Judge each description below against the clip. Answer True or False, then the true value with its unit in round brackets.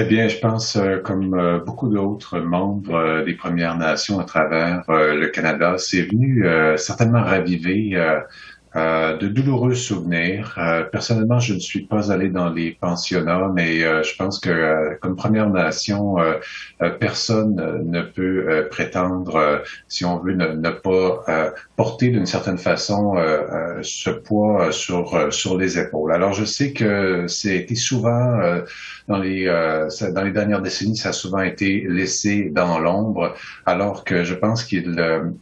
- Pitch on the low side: True (95 Hz)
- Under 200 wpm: True (175 wpm)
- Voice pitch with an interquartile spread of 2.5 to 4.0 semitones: True (3.3 semitones)